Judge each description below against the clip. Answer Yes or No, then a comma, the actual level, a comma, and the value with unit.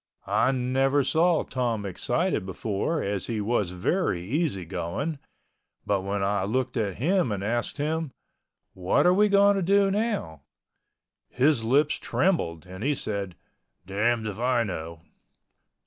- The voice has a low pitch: Yes, low, 120 Hz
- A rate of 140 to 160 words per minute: Yes, average, 145 wpm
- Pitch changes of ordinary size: No, wide, 8.0 semitones